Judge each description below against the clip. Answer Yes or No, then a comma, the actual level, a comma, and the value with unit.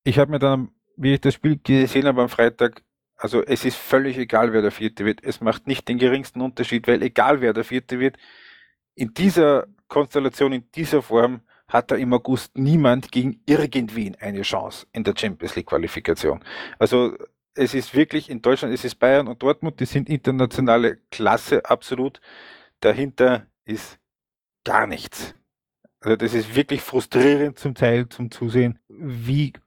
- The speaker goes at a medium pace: Yes, average, 170 wpm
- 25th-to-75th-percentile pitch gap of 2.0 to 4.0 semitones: Yes, average, 2.7 semitones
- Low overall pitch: Yes, low, 130 Hz